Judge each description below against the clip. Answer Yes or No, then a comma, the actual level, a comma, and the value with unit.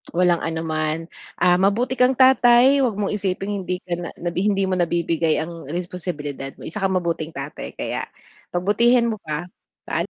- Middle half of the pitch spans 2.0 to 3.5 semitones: No, average, 4.1 semitones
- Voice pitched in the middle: Yes, medium, 180 Hz